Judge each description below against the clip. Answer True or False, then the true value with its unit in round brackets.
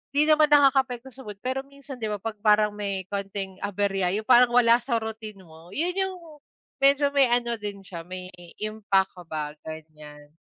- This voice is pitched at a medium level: False (215 Hz)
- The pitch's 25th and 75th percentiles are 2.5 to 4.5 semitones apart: False (5.2 semitones)